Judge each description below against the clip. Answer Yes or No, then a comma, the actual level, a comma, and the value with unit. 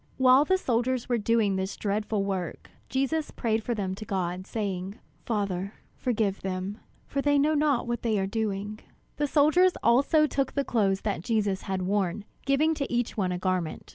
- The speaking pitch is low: No, high, 215 Hz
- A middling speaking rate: Yes, average, 180 wpm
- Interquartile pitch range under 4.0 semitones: No, average, 5.3 semitones